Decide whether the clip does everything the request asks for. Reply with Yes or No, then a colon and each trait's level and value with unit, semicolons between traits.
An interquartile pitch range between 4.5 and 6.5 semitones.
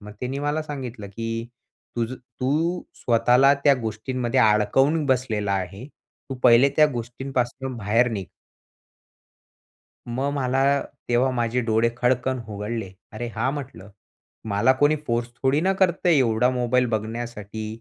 No: average, 2.9 semitones